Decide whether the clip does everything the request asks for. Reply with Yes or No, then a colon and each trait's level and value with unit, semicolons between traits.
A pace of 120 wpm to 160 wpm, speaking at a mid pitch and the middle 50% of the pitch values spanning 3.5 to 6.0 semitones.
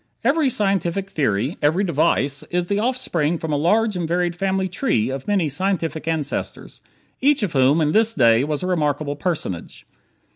No: average, 170 wpm; medium, 170 Hz; average, 5.1 semitones